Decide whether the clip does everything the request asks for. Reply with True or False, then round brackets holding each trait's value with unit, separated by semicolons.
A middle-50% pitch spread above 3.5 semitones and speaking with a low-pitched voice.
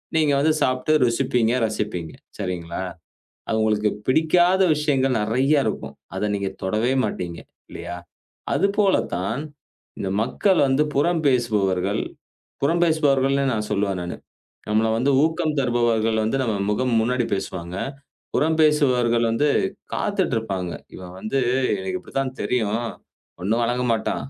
True (4.8 semitones; 120 Hz)